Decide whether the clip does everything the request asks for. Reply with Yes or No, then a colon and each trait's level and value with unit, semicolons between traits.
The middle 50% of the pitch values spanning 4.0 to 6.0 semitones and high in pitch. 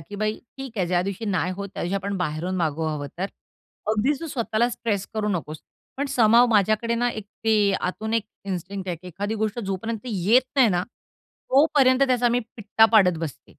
Yes: average, 4.3 semitones; high, 210 Hz